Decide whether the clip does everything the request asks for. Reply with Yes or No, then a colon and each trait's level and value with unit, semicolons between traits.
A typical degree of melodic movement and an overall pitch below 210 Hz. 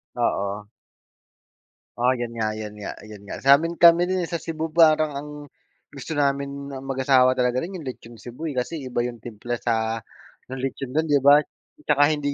Yes: average, 4.3 semitones; low, 135 Hz